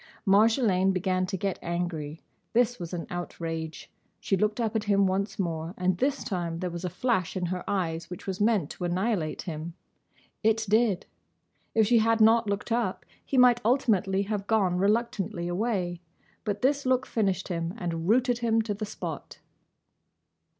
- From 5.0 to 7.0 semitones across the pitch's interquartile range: No, average, 4.2 semitones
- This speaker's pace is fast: No, average, 170 wpm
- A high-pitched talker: Yes, high, 195 Hz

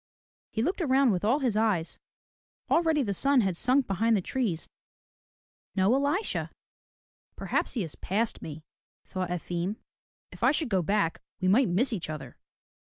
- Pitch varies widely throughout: Yes, wide, 6.6 semitones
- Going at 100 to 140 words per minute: No, average, 155 wpm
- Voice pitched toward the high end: Yes, high, 215 Hz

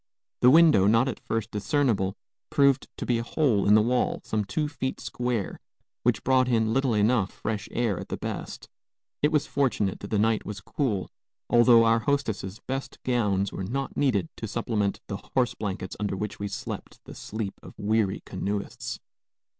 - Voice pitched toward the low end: Yes, low, 110 Hz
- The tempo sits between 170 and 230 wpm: Yes, average, 180 wpm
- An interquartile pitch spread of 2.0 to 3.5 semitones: No, average, 4.0 semitones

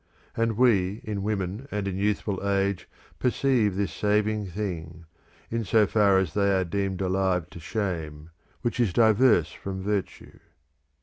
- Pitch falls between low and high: No, low, 100 Hz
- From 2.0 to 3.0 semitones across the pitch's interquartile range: Yes, narrow, 2.5 semitones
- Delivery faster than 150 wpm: No, average, 145 wpm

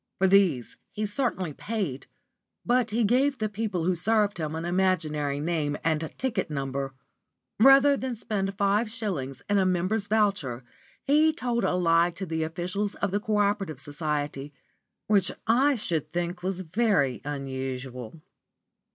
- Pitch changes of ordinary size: No, wide, 5.9 semitones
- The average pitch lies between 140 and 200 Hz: Yes, medium, 185 Hz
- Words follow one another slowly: No, average, 150 wpm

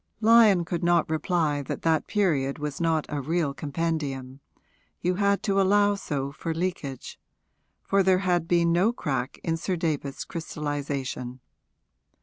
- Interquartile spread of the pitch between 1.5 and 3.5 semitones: No, average, 4.2 semitones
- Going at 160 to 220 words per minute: No, average, 140 wpm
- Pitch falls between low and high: Yes, medium, 165 Hz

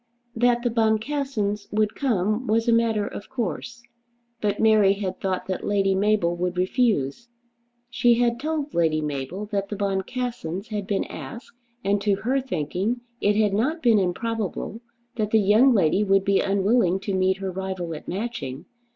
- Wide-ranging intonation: No, average, 3.5 semitones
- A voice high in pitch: Yes, high, 205 Hz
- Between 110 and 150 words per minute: No, average, 165 wpm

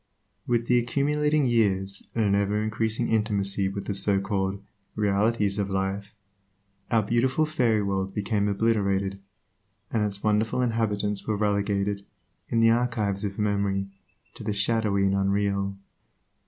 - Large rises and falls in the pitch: No, narrow, 2.4 semitones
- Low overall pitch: Yes, low, 105 Hz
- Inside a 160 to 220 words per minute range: No, average, 140 wpm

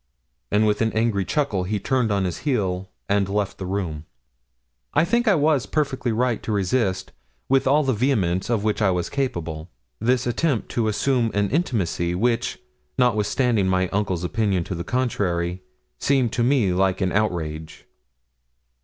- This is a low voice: Yes, low, 105 Hz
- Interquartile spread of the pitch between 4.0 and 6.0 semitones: Yes, average, 5.2 semitones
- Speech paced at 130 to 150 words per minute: No, average, 160 wpm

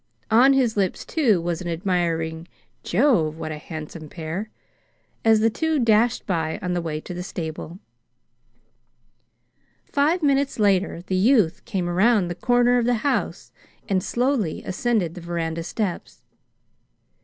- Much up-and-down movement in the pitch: Yes, wide, 6.0 semitones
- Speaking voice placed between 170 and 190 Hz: Yes, medium, 185 Hz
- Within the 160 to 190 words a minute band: No, average, 145 wpm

